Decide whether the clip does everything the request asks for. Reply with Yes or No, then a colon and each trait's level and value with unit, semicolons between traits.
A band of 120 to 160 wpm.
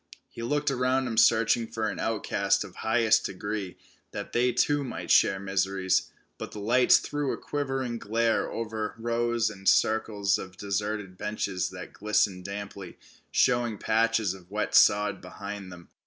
Yes: average, 155 wpm